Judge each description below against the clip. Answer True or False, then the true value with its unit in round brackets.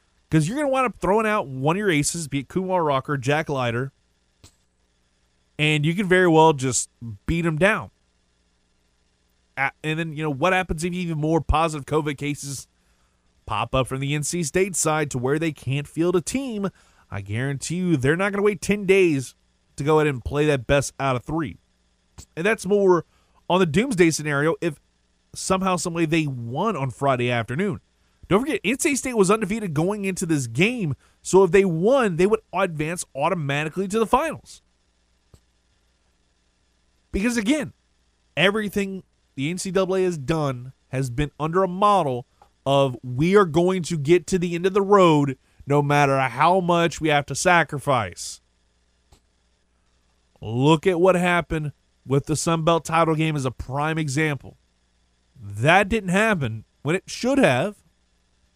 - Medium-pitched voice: True (150 Hz)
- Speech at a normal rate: True (165 wpm)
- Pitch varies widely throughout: True (8.2 semitones)